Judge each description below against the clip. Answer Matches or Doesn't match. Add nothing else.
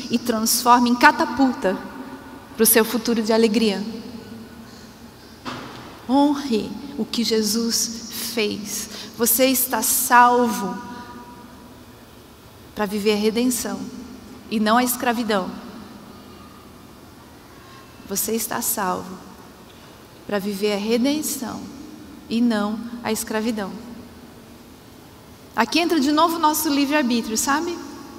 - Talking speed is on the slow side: Matches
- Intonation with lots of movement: Doesn't match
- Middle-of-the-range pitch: Doesn't match